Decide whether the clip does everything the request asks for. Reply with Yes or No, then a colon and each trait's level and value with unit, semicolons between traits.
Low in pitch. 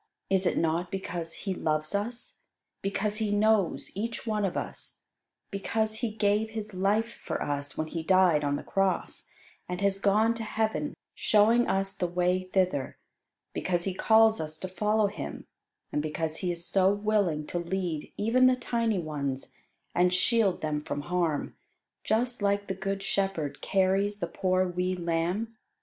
No: high, 195 Hz